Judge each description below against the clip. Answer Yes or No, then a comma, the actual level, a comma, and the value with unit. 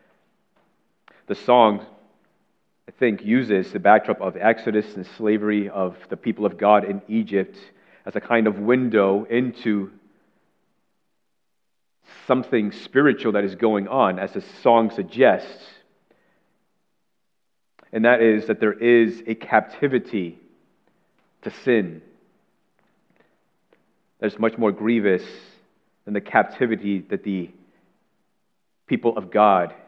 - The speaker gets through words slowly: Yes, slow, 115 wpm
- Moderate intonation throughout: No, narrow, 2.2 semitones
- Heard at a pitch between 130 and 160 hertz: No, low, 105 Hz